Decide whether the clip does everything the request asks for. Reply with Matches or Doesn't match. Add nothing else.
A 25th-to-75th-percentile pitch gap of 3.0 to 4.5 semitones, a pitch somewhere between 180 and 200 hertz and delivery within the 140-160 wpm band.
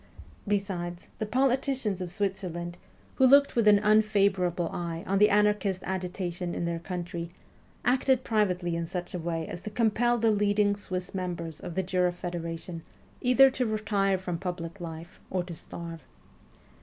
Matches